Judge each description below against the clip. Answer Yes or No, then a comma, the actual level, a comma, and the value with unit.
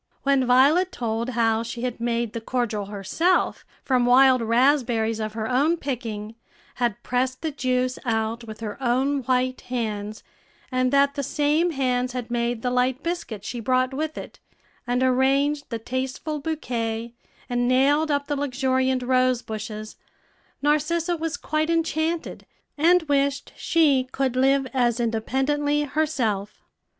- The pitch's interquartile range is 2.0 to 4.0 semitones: Yes, average, 3.4 semitones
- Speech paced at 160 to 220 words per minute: No, average, 140 wpm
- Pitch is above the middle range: Yes, very high, 255 Hz